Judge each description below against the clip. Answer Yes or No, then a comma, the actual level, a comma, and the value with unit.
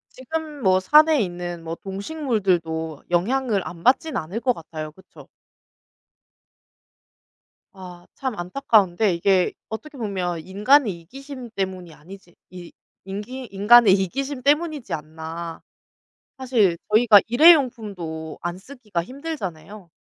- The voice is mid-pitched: No, high, 200 Hz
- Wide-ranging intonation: Yes, wide, 6.7 semitones